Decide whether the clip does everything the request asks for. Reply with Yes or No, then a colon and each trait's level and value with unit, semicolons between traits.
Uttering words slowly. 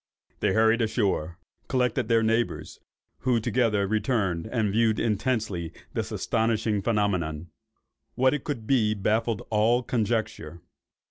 Yes: slow, 120 wpm